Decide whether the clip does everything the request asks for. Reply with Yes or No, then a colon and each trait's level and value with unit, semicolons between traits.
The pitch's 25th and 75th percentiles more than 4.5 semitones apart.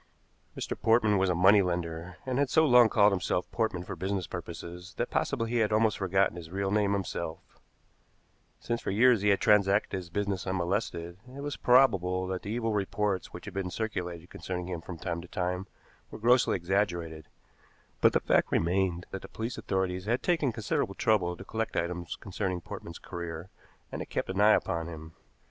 No: average, 3.5 semitones